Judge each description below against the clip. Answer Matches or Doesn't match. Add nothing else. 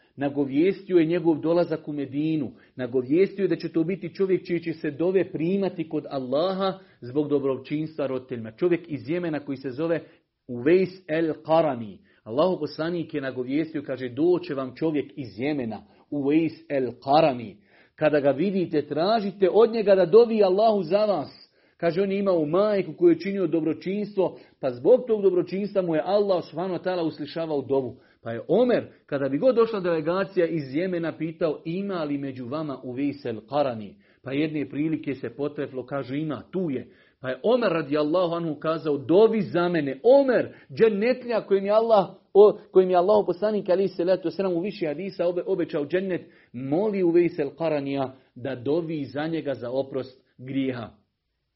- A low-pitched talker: Doesn't match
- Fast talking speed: Matches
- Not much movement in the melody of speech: Doesn't match